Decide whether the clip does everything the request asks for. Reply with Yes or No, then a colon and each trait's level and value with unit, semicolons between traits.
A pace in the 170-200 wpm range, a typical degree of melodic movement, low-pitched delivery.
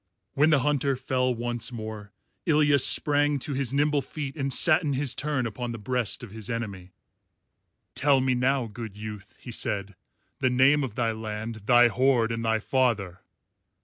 Yes: average, 175 wpm; average, 3.8 semitones; low, 125 Hz